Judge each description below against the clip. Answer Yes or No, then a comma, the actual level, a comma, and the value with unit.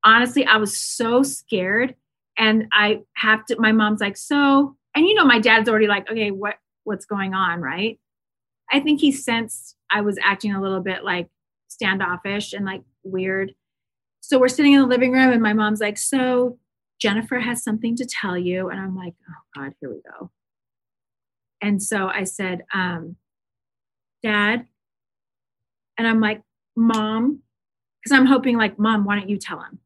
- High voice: Yes, high, 210 Hz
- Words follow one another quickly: No, average, 175 wpm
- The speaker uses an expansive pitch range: No, average, 4.0 semitones